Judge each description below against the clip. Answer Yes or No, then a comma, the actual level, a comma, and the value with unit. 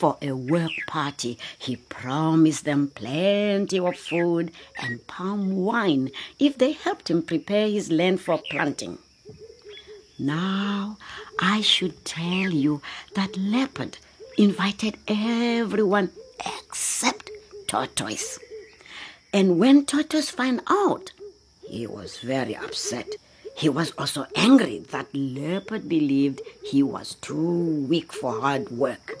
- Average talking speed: No, slow, 115 wpm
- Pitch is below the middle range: No, high, 195 Hz